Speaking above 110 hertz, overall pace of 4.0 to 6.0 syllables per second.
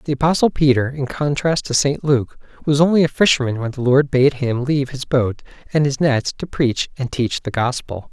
Yes: low, 135 Hz; 5.1 syllables/s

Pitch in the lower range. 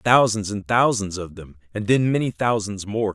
Yes: low, 105 Hz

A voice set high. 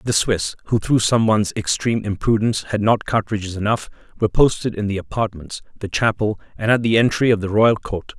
No: low, 105 Hz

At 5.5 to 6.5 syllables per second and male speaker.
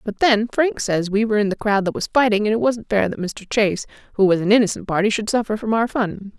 No: 6.1 syllables/s; female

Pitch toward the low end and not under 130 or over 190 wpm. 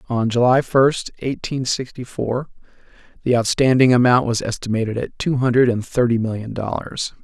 Yes: low, 120 Hz; average, 150 wpm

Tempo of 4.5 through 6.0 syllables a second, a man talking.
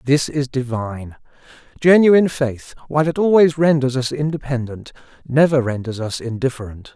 Yes: 5.3 syllables/s; male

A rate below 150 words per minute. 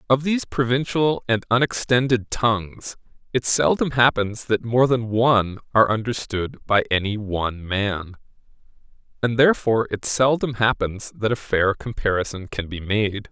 Yes: average, 140 wpm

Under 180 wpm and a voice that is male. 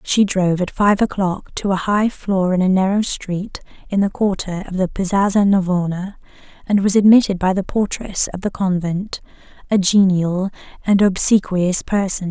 No: average, 165 wpm; female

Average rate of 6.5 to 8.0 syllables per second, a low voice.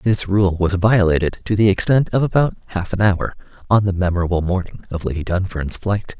No: 5.4 syllables/s; very low, 95 Hz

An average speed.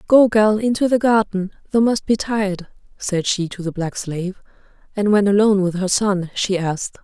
Yes: average, 195 wpm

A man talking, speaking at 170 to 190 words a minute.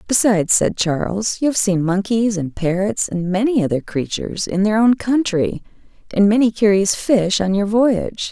No: female; average, 175 wpm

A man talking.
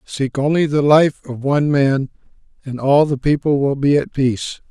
Yes: male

